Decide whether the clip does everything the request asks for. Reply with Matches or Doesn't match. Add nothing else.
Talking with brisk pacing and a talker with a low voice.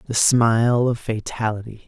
Doesn't match